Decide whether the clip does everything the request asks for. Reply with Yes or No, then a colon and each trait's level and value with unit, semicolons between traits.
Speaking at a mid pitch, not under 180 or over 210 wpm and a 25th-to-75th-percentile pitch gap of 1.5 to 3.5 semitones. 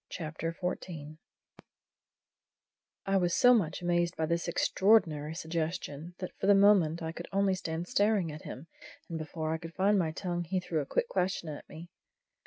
Yes: medium, 170 Hz; average, 190 wpm; average, 2.8 semitones